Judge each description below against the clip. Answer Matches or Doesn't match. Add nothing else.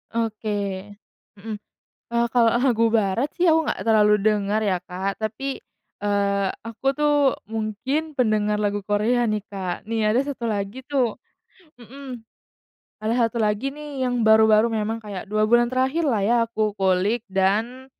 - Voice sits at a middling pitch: Doesn't match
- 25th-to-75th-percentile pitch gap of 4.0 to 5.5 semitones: Doesn't match